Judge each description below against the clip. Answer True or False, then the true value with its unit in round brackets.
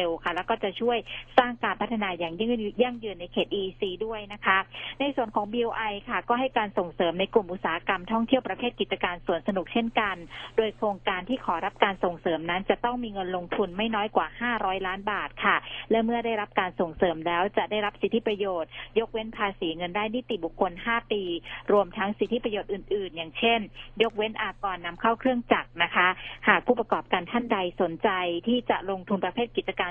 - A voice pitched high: True (205 Hz)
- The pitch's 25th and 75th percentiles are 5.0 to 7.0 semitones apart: False (3.7 semitones)